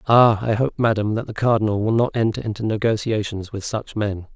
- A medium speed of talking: Yes, average, 195 wpm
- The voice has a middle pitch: No, low, 110 Hz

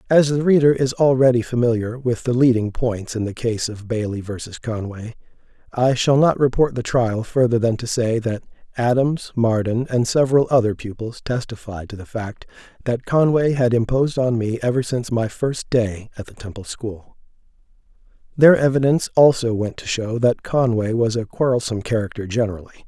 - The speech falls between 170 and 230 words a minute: Yes, average, 175 wpm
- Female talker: No, male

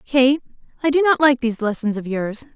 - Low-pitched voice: No, very high, 255 Hz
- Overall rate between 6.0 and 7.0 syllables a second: No, 5.6 syllables/s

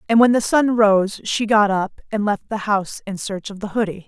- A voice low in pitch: No, high, 210 Hz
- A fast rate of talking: Yes, fast, 250 wpm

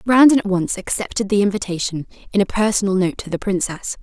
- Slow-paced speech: No, average, 195 wpm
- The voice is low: No, high, 200 Hz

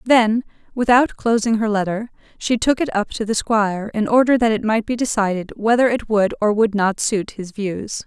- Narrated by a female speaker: Yes, female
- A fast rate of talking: Yes, fast, 210 wpm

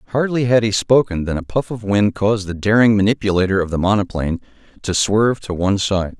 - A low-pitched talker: Yes, low, 100 Hz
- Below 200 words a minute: No, fast, 205 wpm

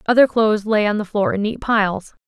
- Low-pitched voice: No, high, 210 Hz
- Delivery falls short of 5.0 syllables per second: No, 6.0 syllables/s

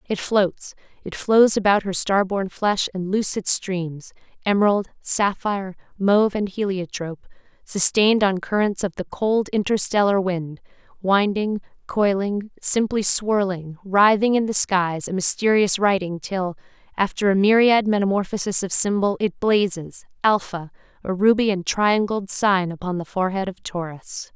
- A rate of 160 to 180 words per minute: No, average, 140 wpm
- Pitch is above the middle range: Yes, high, 195 Hz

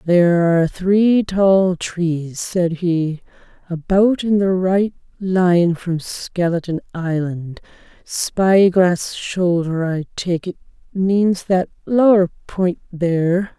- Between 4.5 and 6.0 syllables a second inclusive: No, 3.2 syllables/s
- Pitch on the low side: No, medium, 180 Hz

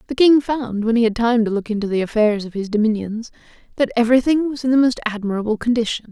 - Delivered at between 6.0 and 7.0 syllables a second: Yes, 6.5 syllables/s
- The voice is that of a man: No, female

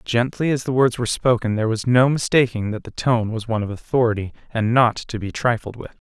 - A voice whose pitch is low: Yes, low, 115 Hz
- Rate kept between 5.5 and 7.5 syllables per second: Yes, 6.0 syllables/s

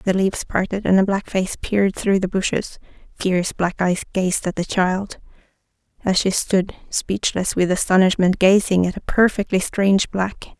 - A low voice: No, high, 190 Hz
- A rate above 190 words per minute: No, average, 170 wpm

